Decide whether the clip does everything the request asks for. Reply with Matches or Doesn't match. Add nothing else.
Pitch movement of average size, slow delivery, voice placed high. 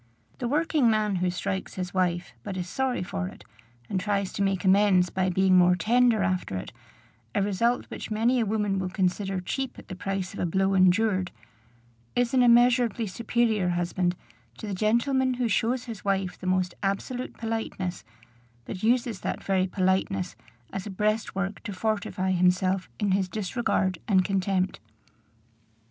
Doesn't match